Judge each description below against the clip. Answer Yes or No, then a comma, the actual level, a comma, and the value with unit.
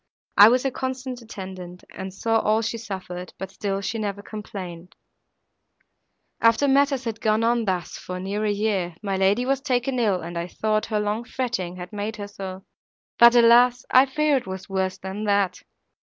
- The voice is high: Yes, high, 210 Hz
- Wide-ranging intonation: No, average, 3.8 semitones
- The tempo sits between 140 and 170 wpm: No, average, 180 wpm